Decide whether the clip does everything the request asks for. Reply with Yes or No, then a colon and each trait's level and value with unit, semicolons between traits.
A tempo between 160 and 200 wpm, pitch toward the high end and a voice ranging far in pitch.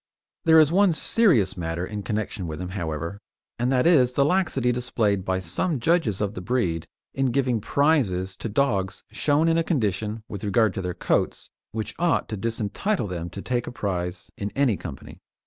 No: average, 185 wpm; low, 110 Hz; wide, 6.8 semitones